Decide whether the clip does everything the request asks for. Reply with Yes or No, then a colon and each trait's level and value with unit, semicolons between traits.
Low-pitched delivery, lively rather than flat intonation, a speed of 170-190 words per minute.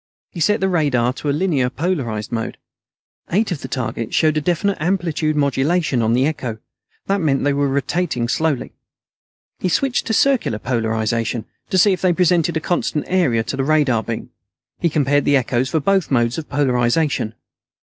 No: medium, 145 Hz; wide, 6.0 semitones; average, 180 wpm